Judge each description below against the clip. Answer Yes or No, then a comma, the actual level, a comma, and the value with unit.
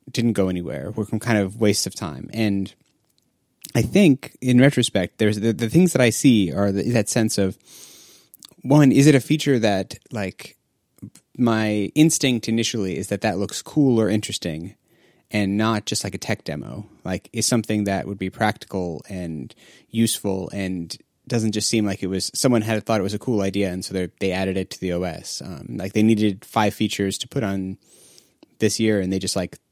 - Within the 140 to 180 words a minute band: No, average, 200 wpm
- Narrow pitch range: No, average, 3.0 semitones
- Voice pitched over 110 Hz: No, low, 105 Hz